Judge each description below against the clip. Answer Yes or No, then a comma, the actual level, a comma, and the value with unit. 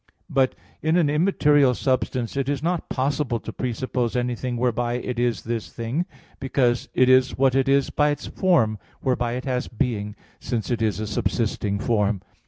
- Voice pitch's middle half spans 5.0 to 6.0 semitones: No, average, 2.9 semitones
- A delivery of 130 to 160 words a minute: No, average, 175 wpm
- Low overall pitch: Yes, low, 125 Hz